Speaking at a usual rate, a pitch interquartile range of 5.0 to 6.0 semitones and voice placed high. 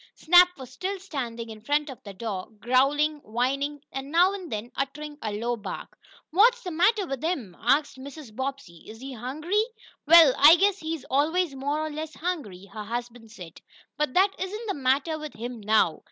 Yes: average, 185 wpm; wide, 5.5 semitones; very high, 280 Hz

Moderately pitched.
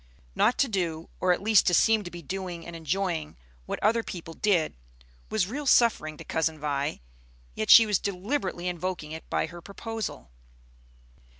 Yes: medium, 180 Hz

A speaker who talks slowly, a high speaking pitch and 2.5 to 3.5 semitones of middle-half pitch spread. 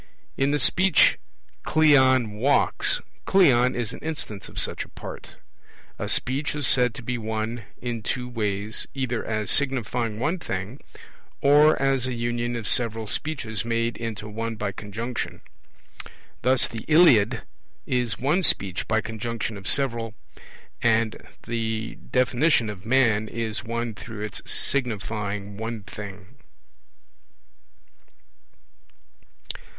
No: slow, 125 wpm; low, 115 Hz; average, 3.0 semitones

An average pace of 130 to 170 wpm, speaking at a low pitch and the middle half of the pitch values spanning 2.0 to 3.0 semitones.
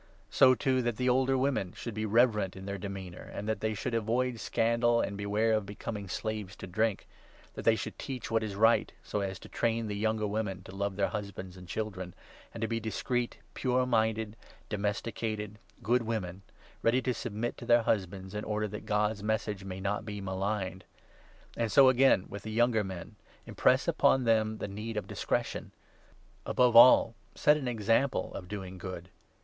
No: average, 195 wpm; low, 110 Hz; average, 2.7 semitones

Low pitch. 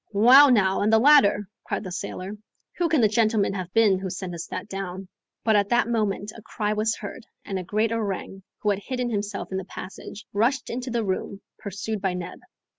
No: high, 210 Hz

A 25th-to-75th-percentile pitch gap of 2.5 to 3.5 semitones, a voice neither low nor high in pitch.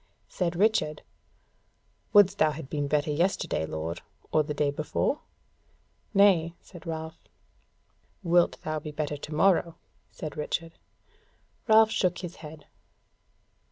Yes: average, 3.0 semitones; medium, 160 Hz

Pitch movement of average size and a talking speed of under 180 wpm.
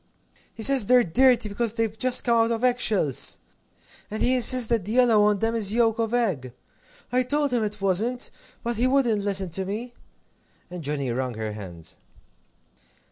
No: average, 4.1 semitones; average, 185 wpm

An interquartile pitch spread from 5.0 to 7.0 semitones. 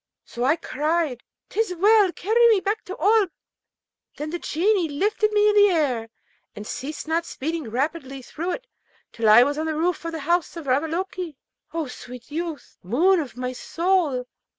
Yes: wide, 5.5 semitones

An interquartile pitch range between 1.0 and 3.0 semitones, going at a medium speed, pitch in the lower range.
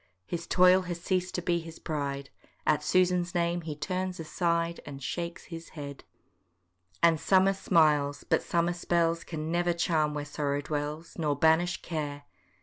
No: average, 2.7 semitones; average, 155 wpm; medium, 165 Hz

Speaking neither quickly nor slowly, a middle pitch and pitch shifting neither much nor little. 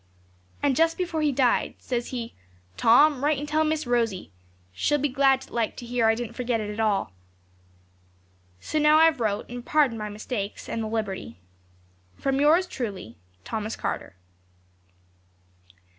No: average, 150 wpm; high, 245 Hz; average, 5.0 semitones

